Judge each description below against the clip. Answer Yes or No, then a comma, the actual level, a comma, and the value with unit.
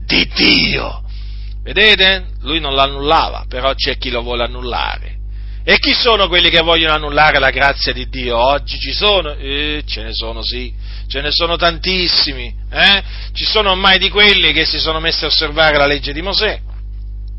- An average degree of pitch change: No, wide, 6.3 semitones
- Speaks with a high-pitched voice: No, medium, 140 Hz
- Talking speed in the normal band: No, fast, 175 wpm